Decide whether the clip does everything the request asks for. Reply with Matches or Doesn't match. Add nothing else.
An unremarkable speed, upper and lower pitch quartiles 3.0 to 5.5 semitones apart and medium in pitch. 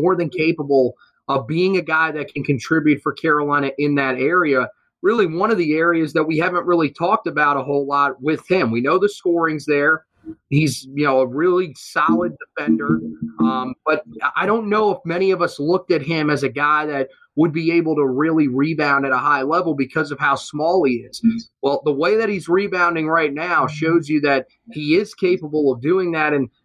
Doesn't match